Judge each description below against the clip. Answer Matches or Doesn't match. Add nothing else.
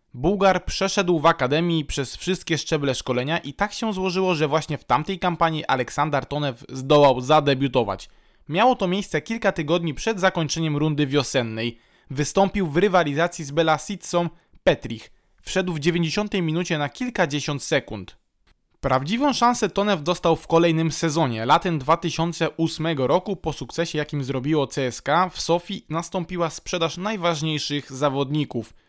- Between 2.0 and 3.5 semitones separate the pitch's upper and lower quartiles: Doesn't match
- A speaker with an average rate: Matches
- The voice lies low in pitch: Doesn't match